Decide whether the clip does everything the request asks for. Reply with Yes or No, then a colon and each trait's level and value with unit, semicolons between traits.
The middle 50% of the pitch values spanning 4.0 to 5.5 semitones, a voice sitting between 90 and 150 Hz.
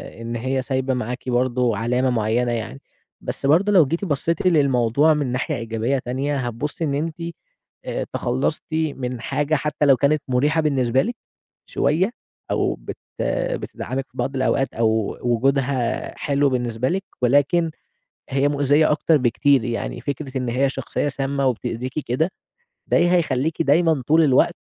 No: average, 3.4 semitones; low, 135 Hz